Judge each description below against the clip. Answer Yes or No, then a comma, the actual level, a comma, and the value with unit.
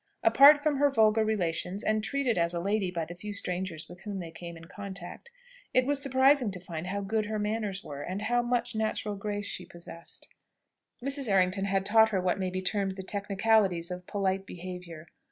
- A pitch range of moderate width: Yes, average, 3.4 semitones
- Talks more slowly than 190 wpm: No, average, 200 wpm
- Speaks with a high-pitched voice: Yes, high, 200 Hz